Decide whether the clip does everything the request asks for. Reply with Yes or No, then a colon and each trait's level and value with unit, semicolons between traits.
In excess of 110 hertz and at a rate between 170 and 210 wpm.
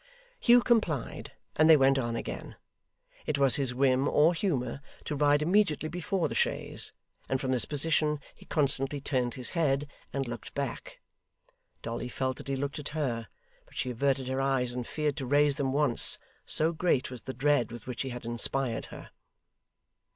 Yes: medium, 140 Hz; average, 180 wpm